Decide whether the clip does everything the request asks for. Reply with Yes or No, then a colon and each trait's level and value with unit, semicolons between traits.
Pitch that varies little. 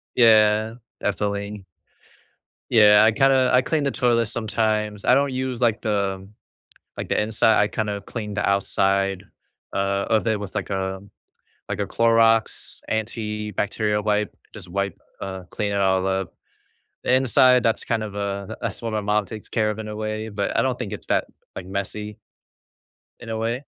Yes: narrow, 2.1 semitones